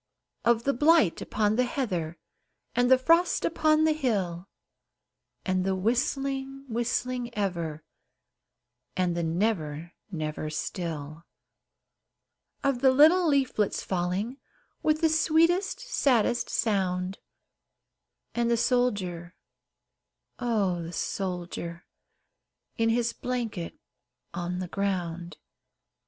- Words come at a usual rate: No, slow, 100 wpm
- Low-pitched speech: No, high, 215 Hz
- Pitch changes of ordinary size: No, wide, 6.8 semitones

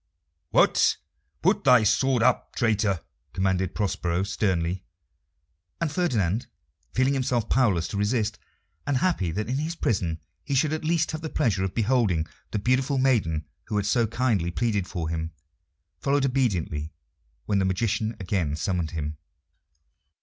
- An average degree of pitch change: No, wide, 6.2 semitones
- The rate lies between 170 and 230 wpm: No, average, 145 wpm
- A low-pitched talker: Yes, low, 105 Hz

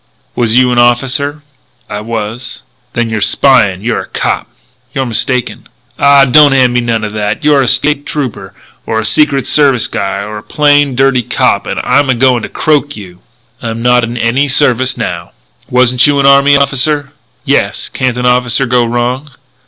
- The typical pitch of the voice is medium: No, low, 125 Hz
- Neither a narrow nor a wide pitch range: Yes, average, 3.0 semitones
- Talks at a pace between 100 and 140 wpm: No, average, 180 wpm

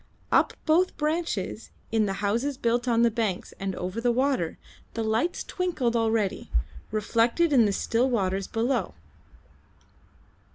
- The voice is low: No, high, 230 Hz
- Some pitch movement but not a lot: Yes, average, 3.9 semitones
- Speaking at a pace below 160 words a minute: Yes, slow, 135 wpm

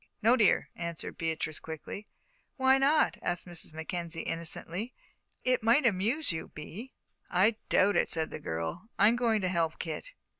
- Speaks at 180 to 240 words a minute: No, average, 155 wpm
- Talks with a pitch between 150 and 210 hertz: Yes, medium, 185 Hz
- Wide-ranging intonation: Yes, wide, 6.3 semitones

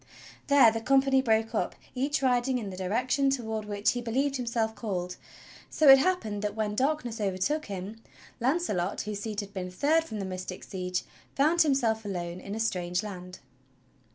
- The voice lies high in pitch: Yes, high, 220 Hz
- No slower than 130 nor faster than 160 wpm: No, average, 175 wpm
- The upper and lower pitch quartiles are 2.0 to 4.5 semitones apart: No, average, 5.3 semitones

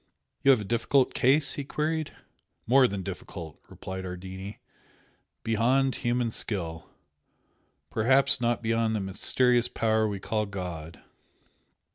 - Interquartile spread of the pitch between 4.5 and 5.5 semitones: Yes, average, 5.0 semitones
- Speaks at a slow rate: Yes, slow, 120 wpm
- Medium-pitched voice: No, low, 110 Hz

